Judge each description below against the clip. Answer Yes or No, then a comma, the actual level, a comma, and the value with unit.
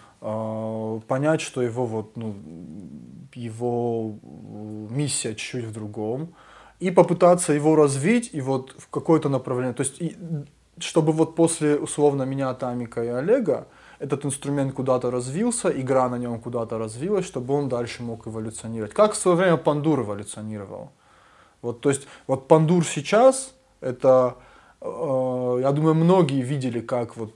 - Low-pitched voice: Yes, low, 130 Hz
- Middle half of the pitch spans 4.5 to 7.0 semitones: Yes, average, 4.9 semitones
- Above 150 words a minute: No, average, 140 wpm